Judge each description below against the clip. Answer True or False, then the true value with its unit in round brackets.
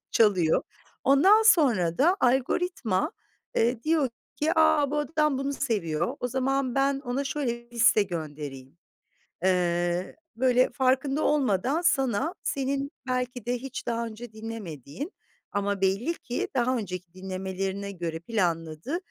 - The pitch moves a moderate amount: False (6.5 semitones)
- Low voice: False (240 Hz)